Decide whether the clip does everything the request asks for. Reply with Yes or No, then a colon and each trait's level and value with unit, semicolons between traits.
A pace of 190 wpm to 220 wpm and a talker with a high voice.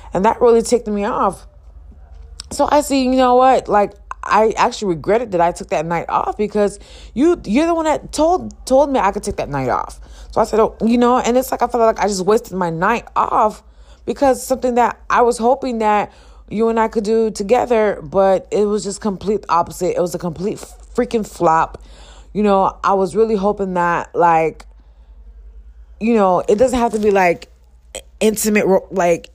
Yes: average, 200 wpm; high, 210 Hz